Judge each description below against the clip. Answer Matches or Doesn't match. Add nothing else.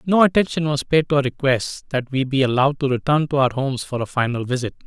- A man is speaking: Matches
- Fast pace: Matches